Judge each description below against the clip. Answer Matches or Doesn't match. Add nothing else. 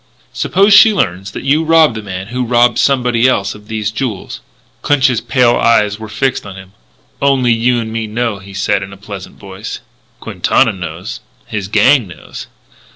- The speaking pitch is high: Doesn't match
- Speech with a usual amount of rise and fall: Matches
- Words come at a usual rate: Matches